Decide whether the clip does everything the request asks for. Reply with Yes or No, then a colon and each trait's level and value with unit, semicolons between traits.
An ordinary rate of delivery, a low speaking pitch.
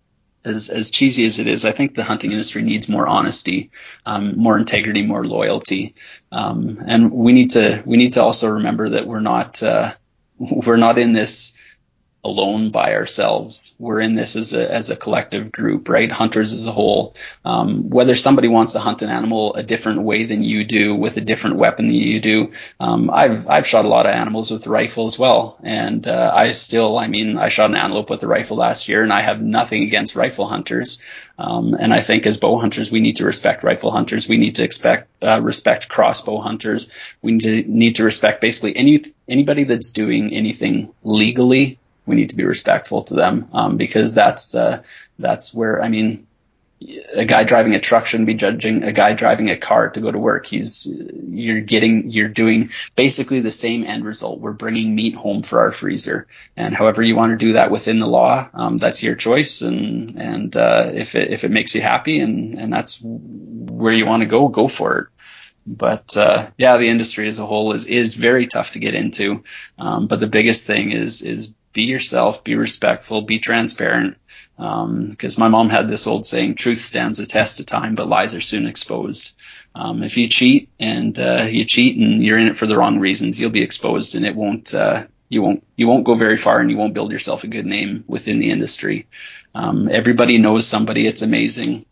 No: fast, 210 wpm; low, 115 Hz